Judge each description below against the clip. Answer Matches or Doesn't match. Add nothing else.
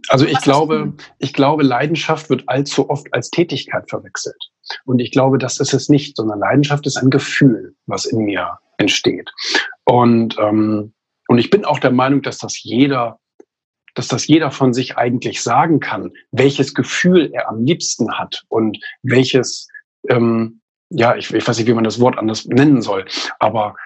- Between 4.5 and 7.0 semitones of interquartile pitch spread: Doesn't match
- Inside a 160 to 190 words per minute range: Matches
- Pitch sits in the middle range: Doesn't match